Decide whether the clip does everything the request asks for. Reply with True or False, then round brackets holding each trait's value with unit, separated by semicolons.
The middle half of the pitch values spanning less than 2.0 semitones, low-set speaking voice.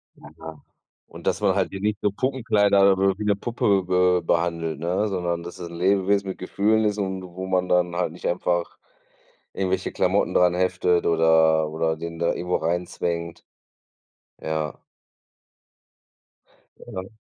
False (2.6 semitones; 90 Hz)